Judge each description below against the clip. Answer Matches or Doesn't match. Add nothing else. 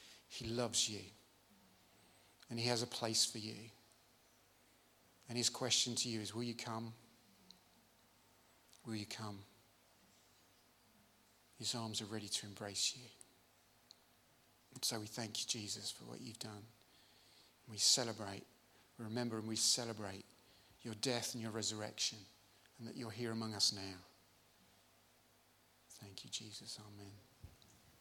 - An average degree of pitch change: Doesn't match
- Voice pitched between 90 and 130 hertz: Matches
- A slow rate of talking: Matches